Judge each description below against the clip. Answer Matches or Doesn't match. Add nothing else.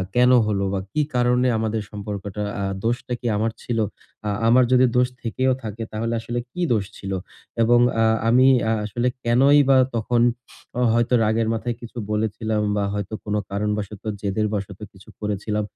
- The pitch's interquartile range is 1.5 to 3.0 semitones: Matches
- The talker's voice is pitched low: Matches